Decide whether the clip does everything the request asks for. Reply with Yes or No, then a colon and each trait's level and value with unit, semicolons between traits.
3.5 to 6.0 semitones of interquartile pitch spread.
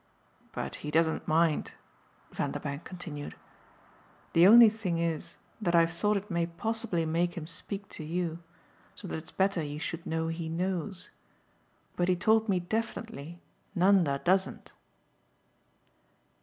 No: average, 3.1 semitones